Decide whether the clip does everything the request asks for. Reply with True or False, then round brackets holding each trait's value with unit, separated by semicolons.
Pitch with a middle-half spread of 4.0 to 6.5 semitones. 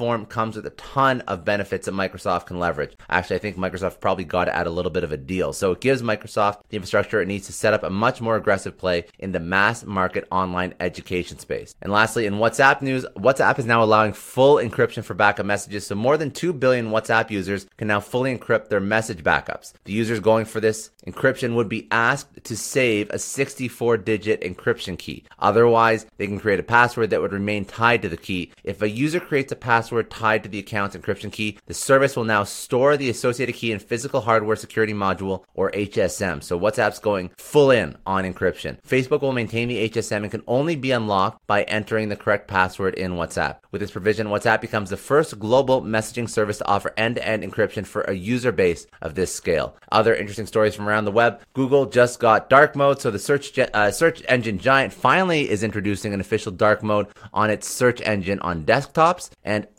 False (3.0 semitones)